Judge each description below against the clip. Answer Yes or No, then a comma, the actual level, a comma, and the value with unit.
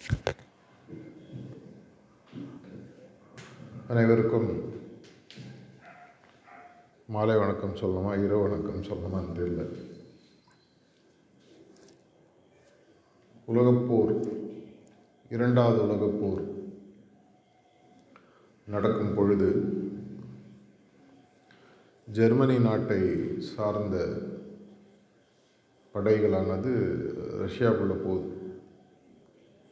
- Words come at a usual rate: No, slow, 45 wpm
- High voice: No, low, 105 Hz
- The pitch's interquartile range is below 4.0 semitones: Yes, average, 2.9 semitones